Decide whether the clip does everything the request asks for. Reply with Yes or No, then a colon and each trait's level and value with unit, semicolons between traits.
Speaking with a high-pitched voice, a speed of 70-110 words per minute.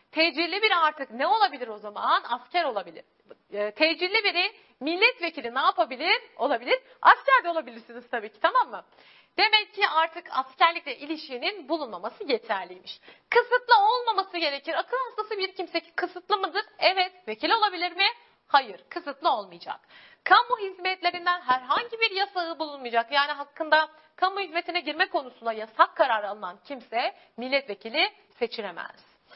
No: very high, 340 Hz; average, 130 wpm